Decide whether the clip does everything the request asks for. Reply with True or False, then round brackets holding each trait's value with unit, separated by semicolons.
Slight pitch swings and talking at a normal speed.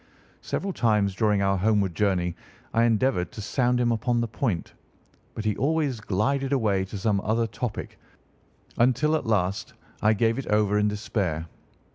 False (3.5 semitones; 160 wpm)